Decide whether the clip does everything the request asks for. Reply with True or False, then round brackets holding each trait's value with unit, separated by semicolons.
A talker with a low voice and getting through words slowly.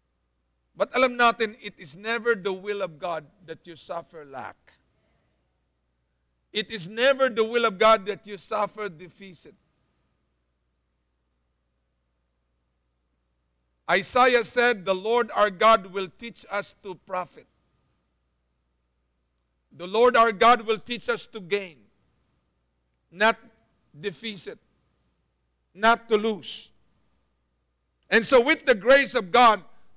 False (185 Hz; 110 wpm)